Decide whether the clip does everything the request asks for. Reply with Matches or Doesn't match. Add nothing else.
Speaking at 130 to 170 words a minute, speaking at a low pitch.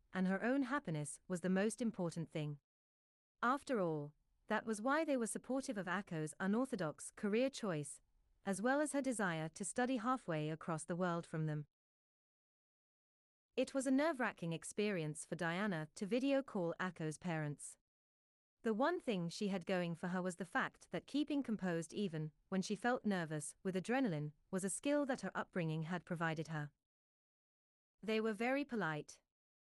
Doesn't match